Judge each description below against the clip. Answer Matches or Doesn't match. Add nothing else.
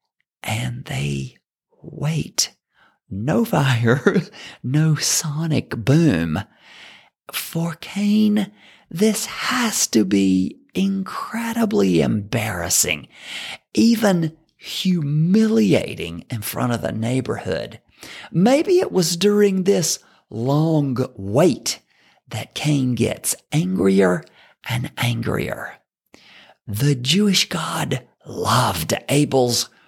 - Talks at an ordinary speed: Doesn't match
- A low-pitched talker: Doesn't match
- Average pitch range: Doesn't match